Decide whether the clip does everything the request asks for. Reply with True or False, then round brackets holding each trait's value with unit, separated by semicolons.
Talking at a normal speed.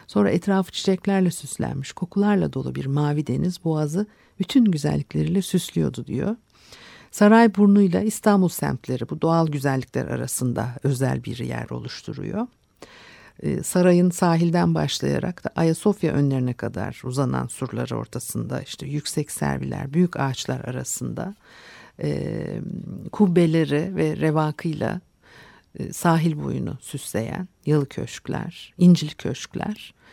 True (105 wpm)